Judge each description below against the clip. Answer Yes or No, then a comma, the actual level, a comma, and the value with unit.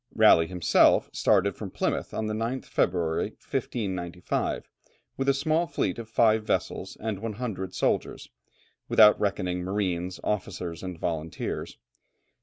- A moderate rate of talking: No, slow, 125 wpm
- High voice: No, very low, 95 Hz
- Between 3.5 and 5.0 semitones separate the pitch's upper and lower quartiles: Yes, average, 3.9 semitones